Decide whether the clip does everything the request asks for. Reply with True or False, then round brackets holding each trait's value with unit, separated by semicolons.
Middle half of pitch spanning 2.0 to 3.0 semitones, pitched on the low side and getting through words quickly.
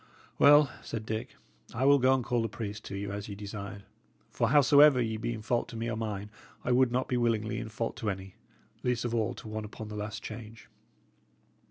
True (2.5 semitones; 115 Hz; 215 wpm)